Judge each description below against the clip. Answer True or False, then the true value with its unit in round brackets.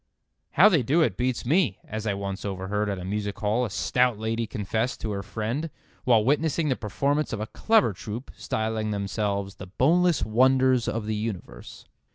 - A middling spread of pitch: True (4.1 semitones)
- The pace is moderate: True (185 wpm)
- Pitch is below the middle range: True (110 Hz)